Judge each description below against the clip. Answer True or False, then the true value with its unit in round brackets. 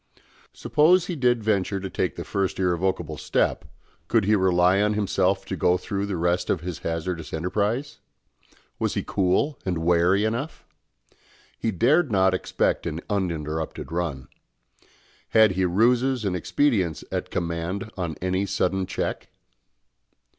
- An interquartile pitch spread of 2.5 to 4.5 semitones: True (3.4 semitones)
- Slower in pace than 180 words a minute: True (140 wpm)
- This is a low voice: True (95 Hz)